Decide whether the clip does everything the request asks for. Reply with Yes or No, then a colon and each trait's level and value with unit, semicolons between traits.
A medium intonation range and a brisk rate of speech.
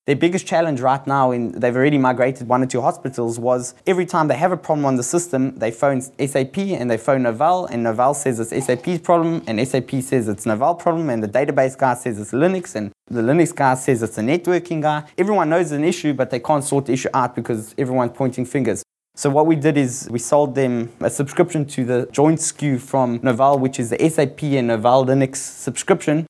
Yes: average, 4.0 semitones; fast, 220 wpm